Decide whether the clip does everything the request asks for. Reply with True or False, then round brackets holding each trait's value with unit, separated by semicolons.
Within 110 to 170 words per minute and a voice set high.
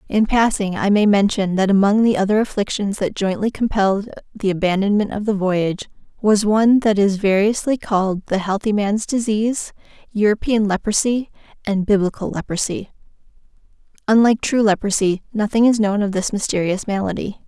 True (150 wpm; 205 Hz)